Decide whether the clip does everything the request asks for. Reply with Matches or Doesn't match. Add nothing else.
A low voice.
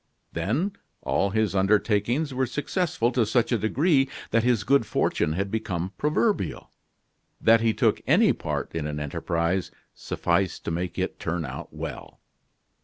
Matches